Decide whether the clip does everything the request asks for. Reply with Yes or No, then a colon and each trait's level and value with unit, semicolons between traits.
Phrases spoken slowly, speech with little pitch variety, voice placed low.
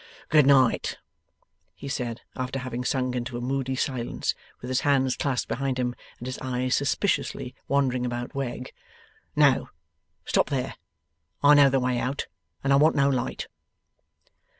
No: average, 150 wpm; narrow, 1.7 semitones; low, 130 Hz